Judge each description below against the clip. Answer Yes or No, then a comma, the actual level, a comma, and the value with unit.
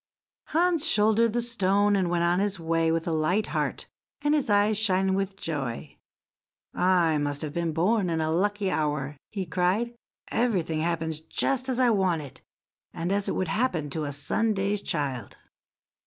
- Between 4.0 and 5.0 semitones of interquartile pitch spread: Yes, average, 4.4 semitones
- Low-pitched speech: No, medium, 185 Hz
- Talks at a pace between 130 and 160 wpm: No, average, 170 wpm